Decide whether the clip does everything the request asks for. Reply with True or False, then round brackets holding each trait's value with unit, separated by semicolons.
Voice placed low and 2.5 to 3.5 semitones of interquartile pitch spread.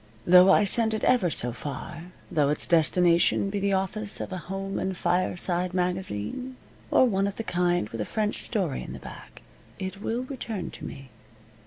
False (185 Hz; 2.9 semitones)